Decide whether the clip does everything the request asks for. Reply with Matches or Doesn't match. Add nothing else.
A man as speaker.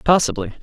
Matches